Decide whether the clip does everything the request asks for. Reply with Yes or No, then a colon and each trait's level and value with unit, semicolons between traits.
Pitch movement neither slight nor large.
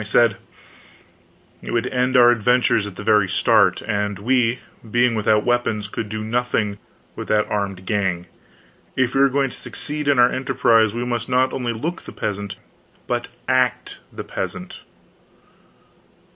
Yes: average, 3.2 semitones